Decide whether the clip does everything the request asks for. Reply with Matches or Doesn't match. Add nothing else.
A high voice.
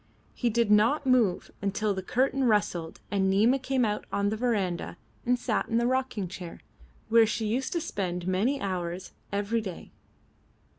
Matches